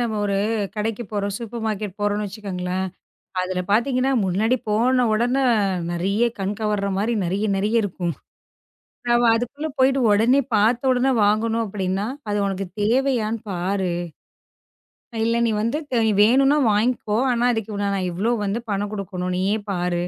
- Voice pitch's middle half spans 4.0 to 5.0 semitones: No, average, 3.3 semitones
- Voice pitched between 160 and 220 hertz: Yes, high, 210 Hz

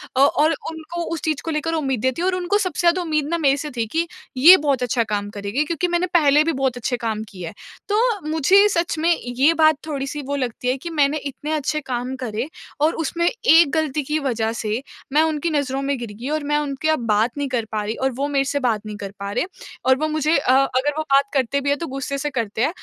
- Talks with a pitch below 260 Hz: No, very high, 280 Hz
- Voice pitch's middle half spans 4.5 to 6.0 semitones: No, average, 3.8 semitones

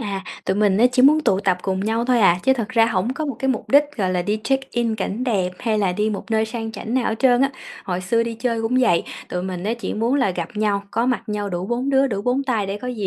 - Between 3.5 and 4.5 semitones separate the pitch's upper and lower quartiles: Yes, average, 4.0 semitones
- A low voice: No, high, 225 Hz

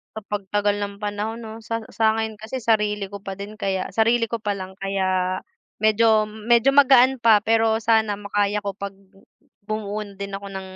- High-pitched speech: Yes, high, 210 Hz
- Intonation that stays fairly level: Yes, narrow, 1.9 semitones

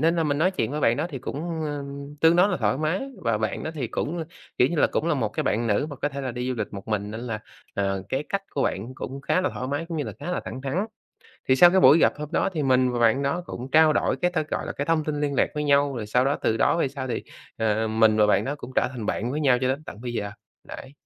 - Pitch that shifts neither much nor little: Yes, average, 4.9 semitones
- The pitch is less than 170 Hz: Yes, low, 135 Hz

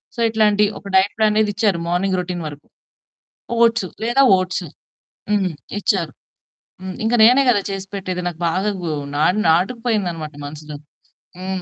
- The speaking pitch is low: No, high, 190 Hz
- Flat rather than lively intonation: No, average, 3.4 semitones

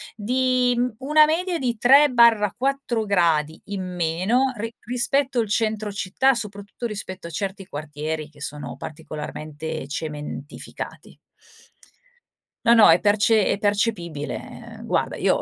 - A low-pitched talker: No, high, 205 Hz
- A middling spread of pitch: No, wide, 7.2 semitones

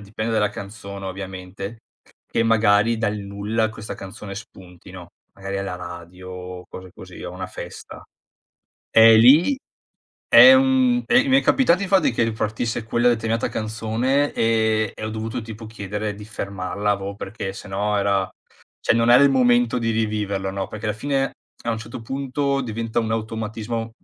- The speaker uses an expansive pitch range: No, average, 2.7 semitones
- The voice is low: Yes, low, 110 Hz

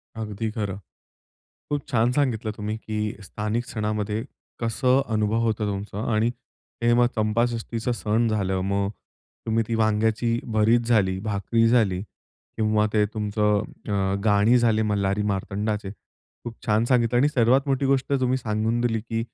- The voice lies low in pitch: Yes, low, 110 Hz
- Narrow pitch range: Yes, narrow, 2.0 semitones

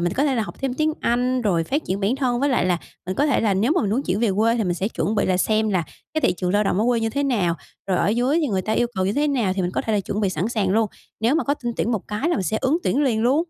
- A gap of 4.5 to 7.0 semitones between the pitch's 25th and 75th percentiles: Yes, average, 4.9 semitones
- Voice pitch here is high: Yes, high, 220 Hz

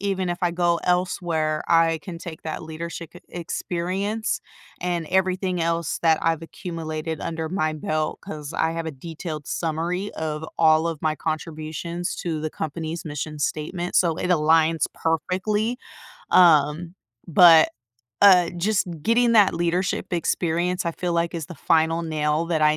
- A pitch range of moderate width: No, narrow, 2.1 semitones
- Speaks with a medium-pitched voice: Yes, medium, 165 Hz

